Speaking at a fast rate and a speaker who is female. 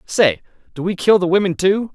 No: fast, 215 wpm; male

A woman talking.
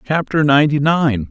No: male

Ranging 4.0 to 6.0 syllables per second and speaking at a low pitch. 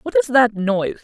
No: 5.4 syllables/s; high, 220 Hz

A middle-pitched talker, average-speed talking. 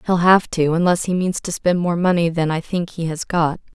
No: medium, 170 Hz; fast, 255 wpm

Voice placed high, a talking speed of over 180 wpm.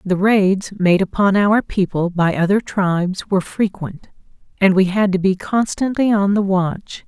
No: high, 195 Hz; average, 170 wpm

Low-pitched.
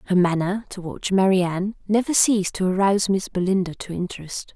No: high, 190 Hz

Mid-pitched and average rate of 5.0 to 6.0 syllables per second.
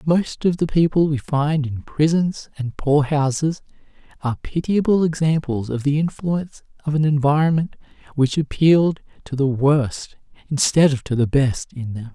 No: medium, 145 Hz; 4.7 syllables/s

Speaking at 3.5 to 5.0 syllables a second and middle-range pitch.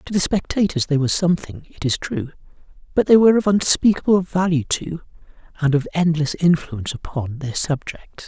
No: 5.5 syllables/s; medium, 160 Hz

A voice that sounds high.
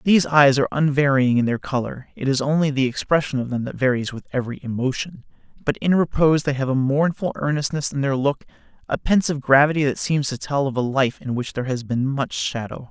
No: medium, 140 Hz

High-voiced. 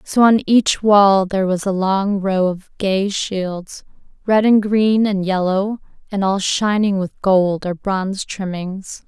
Yes: high, 195 Hz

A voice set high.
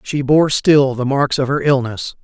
No: low, 135 Hz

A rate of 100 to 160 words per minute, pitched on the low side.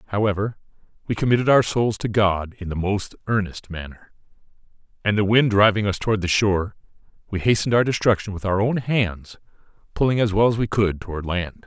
No: average, 185 wpm; low, 100 Hz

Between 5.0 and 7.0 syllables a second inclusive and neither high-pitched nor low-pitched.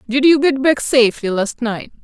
No: 5.1 syllables/s; high, 245 Hz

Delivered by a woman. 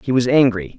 No: male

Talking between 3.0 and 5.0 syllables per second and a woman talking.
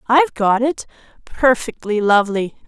Yes: 4.9 syllables/s; female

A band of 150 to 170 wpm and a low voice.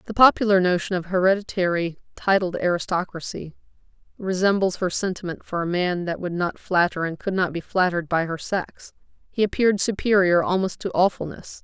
No: average, 160 wpm; medium, 185 Hz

